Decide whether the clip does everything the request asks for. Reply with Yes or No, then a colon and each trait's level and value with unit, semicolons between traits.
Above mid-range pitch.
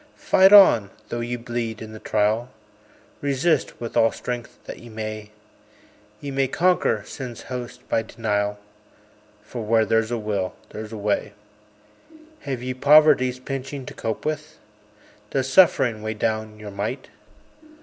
No: low, 120 Hz